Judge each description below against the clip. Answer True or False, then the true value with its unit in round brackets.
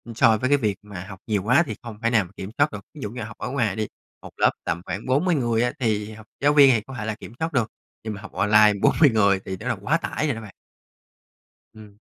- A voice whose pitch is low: True (110 Hz)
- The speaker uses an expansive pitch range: False (3.8 semitones)